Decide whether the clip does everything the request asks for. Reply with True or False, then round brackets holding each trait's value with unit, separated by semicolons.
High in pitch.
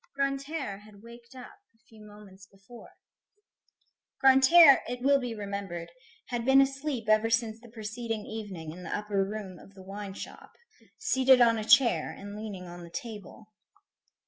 True (220 Hz)